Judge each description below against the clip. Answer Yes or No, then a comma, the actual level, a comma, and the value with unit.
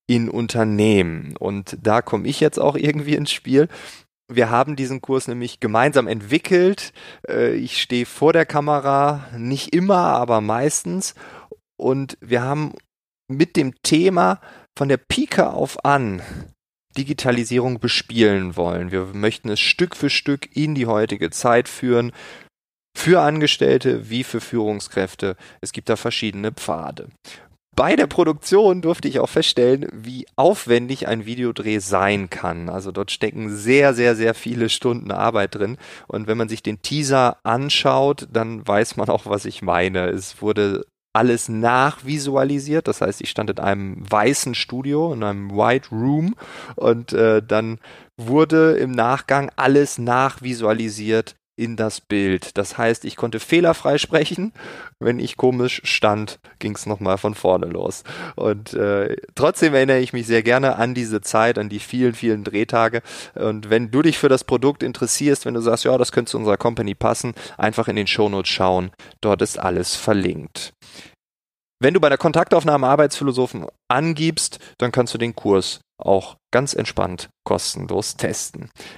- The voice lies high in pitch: No, low, 120 Hz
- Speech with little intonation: No, average, 4.7 semitones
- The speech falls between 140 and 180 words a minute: Yes, average, 155 wpm